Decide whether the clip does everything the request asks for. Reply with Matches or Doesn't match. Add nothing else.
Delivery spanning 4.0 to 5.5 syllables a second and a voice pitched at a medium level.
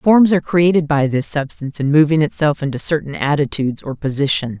Doesn't match